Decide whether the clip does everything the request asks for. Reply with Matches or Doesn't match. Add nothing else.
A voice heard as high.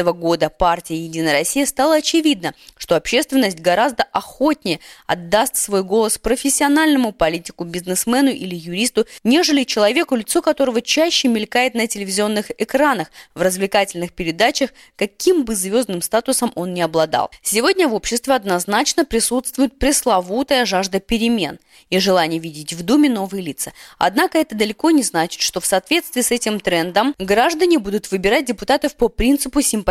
Matches